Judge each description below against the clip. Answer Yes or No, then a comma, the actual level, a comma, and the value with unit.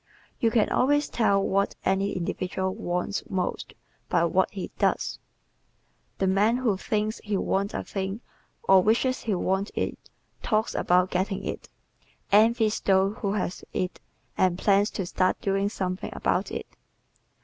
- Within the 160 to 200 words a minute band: No, average, 150 wpm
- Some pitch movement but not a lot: No, narrow, 2.2 semitones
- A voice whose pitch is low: No, high, 195 Hz